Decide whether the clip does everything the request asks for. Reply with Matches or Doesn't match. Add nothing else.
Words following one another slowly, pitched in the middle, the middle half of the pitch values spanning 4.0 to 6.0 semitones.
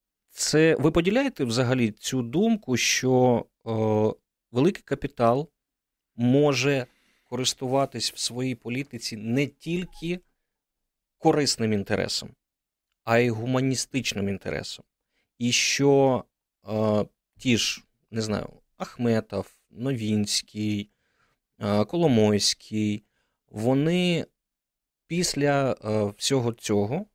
Doesn't match